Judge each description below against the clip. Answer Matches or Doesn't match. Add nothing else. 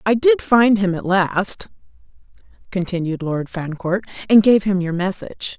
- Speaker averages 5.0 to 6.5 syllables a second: Doesn't match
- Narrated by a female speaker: Matches